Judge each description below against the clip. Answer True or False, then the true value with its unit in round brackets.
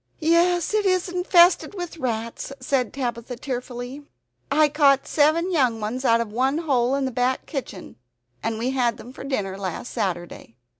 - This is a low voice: False (260 Hz)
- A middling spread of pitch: True (4.6 semitones)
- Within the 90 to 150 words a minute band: False (165 wpm)